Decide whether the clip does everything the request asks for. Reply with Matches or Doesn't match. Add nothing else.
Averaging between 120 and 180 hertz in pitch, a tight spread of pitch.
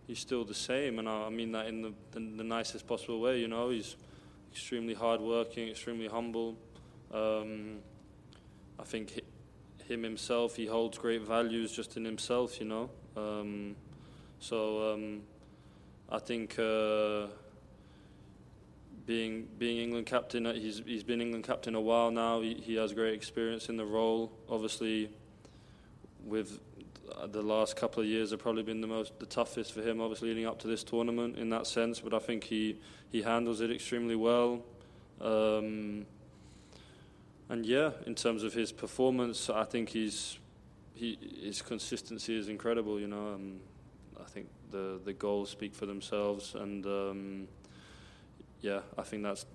Doesn't match